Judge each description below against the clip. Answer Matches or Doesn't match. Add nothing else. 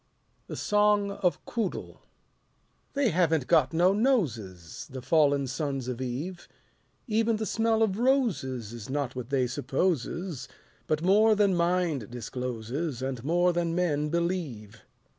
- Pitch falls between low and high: Matches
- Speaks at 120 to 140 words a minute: Matches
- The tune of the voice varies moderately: Doesn't match